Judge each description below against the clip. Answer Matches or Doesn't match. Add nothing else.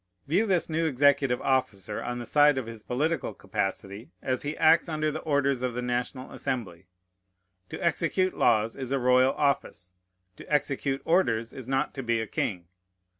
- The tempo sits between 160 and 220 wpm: Matches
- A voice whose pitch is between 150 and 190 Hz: Doesn't match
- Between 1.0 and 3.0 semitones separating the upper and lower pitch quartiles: Doesn't match